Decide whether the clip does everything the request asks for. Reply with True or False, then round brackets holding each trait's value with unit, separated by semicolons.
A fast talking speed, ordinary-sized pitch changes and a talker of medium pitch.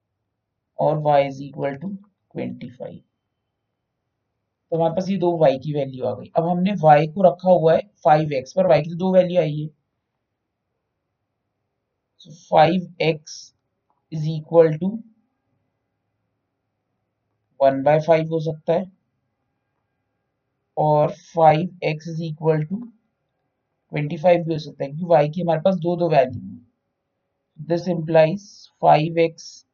False (135 wpm; 4.9 semitones; 150 Hz)